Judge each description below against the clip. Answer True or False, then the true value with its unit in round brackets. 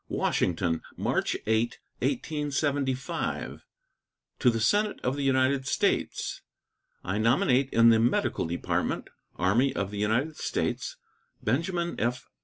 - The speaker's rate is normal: False (115 wpm)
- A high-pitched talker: False (125 Hz)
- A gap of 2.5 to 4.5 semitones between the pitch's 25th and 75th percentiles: True (4.2 semitones)